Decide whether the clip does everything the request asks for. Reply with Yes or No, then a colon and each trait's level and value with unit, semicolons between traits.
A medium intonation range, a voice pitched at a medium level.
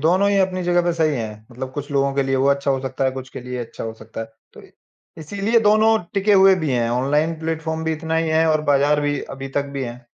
Yes: average, 3.9 semitones; medium, 145 Hz